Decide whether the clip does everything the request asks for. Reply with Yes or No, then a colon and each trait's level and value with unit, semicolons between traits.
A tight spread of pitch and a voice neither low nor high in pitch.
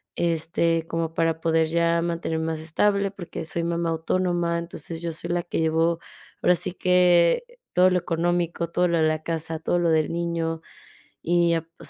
Yes: narrow, 1.0 semitones; medium, 170 Hz